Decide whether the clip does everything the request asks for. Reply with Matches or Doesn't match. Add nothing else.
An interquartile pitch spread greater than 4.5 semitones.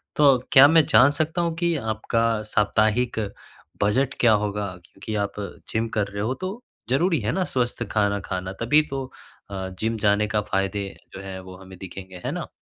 Matches